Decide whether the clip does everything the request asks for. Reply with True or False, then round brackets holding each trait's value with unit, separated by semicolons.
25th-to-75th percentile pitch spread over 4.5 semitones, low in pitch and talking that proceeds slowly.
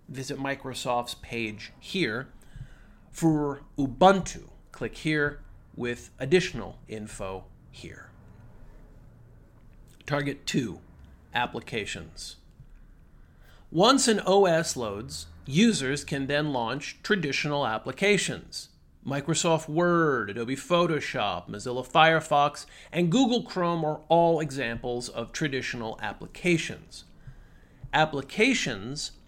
False (5.4 semitones; 145 Hz; 85 wpm)